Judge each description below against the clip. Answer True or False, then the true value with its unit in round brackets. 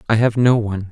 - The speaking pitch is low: True (110 Hz)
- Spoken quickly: True (265 wpm)